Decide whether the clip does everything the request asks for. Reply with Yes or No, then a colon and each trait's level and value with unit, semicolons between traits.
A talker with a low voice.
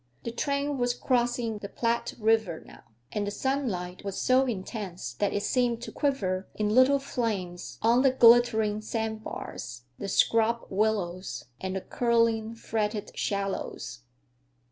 No: high, 220 Hz